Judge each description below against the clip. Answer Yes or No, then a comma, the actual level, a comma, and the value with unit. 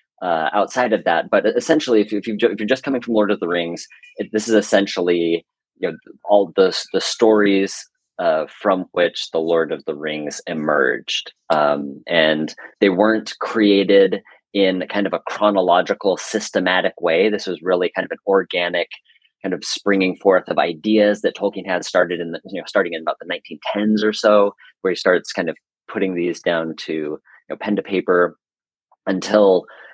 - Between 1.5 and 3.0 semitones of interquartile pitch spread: No, average, 3.5 semitones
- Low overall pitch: Yes, low, 100 Hz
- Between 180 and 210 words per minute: Yes, average, 185 wpm